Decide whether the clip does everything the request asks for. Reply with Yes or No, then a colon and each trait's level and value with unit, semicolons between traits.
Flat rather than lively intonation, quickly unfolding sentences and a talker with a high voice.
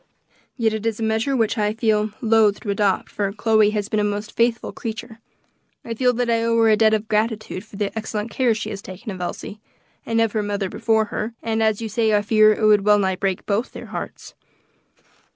Yes: narrow, 1.5 semitones; fast, 220 wpm; high, 215 Hz